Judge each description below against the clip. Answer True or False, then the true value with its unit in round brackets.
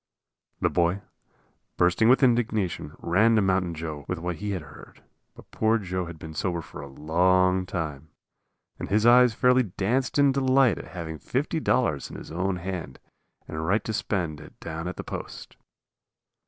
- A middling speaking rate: True (170 wpm)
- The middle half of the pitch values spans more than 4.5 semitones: True (5.3 semitones)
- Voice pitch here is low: True (90 Hz)